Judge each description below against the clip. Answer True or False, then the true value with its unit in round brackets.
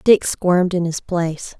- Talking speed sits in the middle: True (190 wpm)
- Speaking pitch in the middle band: True (175 Hz)